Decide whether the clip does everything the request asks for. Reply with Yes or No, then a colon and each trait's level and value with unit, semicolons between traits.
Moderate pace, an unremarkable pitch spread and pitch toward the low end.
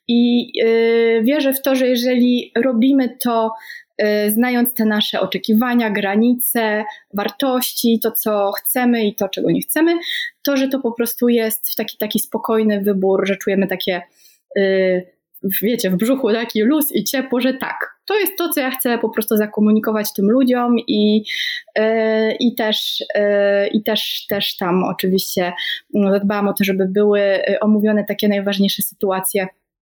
No: average, 145 wpm; average, 3.3 semitones; high, 220 Hz